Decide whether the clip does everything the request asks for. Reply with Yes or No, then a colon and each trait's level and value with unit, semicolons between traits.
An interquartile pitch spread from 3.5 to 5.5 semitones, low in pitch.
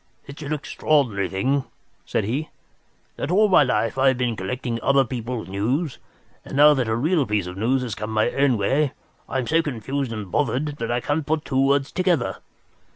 Yes: average, 4.4 semitones; low, 130 Hz